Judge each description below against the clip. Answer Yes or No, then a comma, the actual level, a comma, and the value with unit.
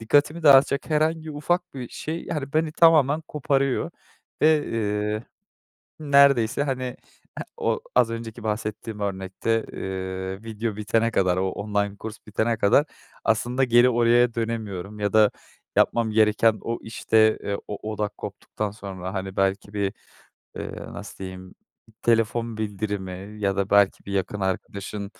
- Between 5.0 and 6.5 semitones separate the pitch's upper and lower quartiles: No, average, 3.8 semitones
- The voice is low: Yes, low, 110 Hz